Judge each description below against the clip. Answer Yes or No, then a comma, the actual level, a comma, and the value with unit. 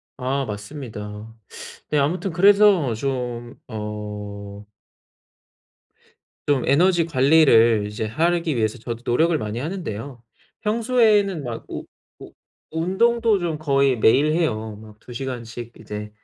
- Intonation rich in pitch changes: Yes, wide, 7.1 semitones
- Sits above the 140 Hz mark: No, low, 130 Hz